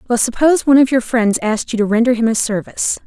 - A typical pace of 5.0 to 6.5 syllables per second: No, 7.1 syllables/s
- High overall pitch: Yes, high, 235 Hz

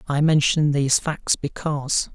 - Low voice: No, medium, 145 Hz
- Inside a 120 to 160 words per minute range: Yes, average, 140 wpm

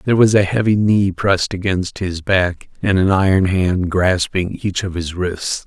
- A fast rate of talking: No, average, 190 wpm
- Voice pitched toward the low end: Yes, very low, 95 Hz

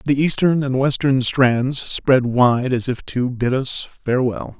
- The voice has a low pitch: Yes, low, 130 Hz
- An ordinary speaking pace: Yes, average, 170 wpm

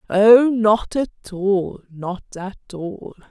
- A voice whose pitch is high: Yes, high, 205 Hz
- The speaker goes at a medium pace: No, slow, 125 wpm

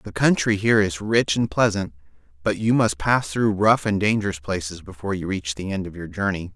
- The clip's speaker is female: No, male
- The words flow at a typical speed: No, fast, 220 wpm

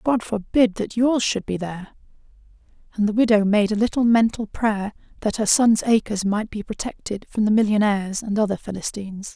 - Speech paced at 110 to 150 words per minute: No, average, 180 wpm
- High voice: Yes, high, 215 Hz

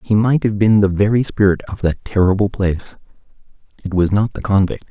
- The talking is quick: No, average, 195 wpm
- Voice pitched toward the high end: No, low, 100 Hz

